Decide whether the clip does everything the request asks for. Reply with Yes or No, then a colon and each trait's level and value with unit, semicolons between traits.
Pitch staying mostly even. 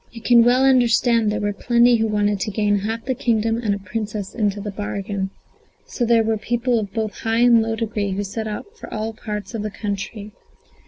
Yes: narrow, 2.2 semitones